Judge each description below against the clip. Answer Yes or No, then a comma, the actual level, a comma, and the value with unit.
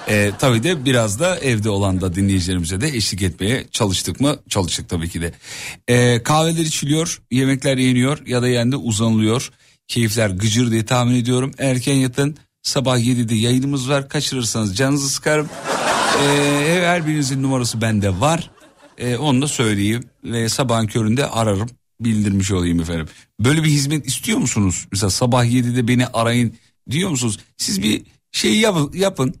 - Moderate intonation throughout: Yes, average, 4.0 semitones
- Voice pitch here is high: No, low, 125 Hz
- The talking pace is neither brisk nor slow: No, fast, 155 wpm